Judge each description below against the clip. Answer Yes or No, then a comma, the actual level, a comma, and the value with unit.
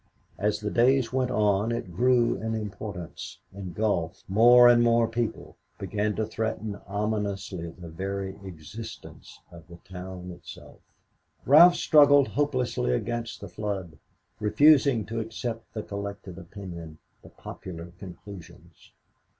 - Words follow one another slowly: Yes, slow, 125 wpm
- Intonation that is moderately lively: Yes, average, 4.0 semitones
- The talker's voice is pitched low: Yes, low, 105 Hz